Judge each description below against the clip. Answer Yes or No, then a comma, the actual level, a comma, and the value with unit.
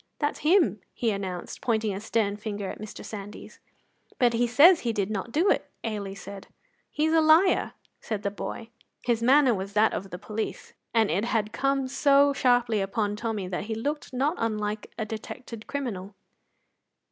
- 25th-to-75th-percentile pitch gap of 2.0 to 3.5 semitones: No, average, 4.2 semitones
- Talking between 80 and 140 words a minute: No, average, 175 wpm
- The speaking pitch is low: No, high, 225 Hz